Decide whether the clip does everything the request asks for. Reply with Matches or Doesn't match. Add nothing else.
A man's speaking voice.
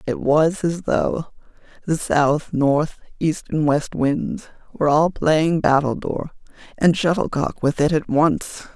Doesn't match